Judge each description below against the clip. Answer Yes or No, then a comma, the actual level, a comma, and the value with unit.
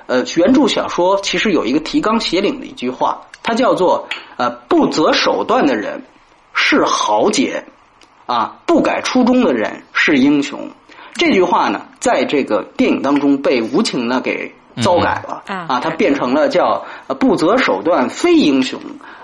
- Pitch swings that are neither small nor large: No, wide, 5.9 semitones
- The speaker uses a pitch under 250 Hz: No, very high, 290 Hz